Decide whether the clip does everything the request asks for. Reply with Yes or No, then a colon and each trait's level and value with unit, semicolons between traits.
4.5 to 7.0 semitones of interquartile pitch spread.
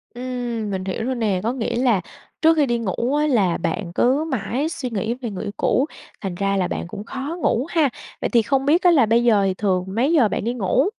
Yes: average, 4.8 semitones